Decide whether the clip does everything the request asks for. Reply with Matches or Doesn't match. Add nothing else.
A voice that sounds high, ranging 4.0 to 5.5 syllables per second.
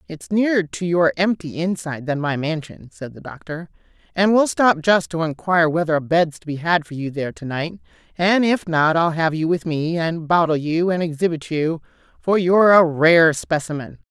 Doesn't match